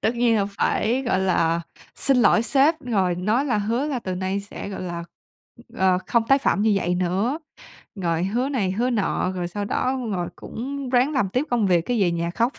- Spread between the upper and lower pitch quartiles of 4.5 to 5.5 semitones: Yes, average, 5.2 semitones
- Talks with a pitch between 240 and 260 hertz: No, high, 210 Hz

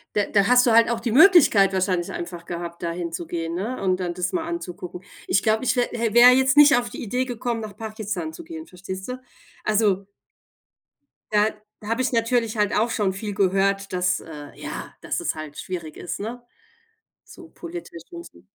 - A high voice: Yes, high, 210 Hz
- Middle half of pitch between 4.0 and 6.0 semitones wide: Yes, average, 5.1 semitones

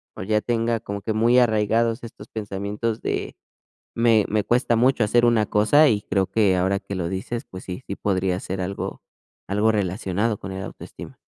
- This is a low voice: Yes, low, 105 Hz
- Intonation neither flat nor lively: Yes, average, 3.1 semitones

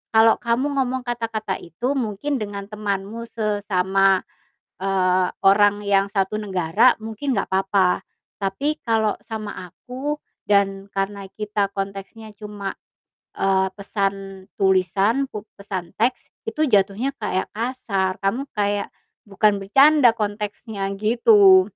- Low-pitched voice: No, high, 205 Hz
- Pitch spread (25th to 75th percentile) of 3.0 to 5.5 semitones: No, narrow, 2.6 semitones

